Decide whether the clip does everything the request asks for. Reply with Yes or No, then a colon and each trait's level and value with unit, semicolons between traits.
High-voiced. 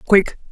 Yes: high, 195 Hz